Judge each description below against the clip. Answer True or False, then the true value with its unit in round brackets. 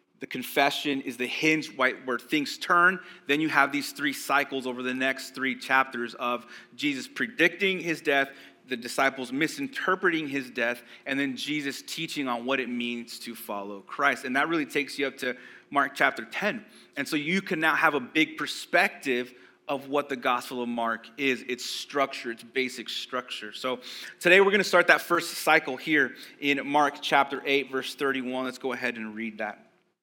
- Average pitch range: True (4.0 semitones)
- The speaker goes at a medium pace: True (185 wpm)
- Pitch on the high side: False (135 Hz)